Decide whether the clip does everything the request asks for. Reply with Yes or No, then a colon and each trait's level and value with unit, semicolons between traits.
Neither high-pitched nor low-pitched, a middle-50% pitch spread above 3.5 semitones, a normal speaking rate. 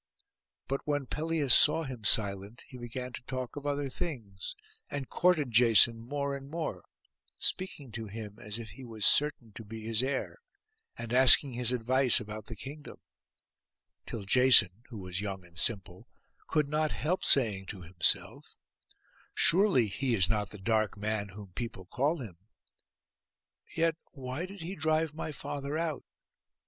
No: low, 125 Hz; wide, 5.4 semitones; average, 155 wpm